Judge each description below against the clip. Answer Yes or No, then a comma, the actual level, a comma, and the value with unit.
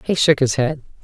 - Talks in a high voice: No, medium, 145 Hz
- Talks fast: Yes, fast, 230 wpm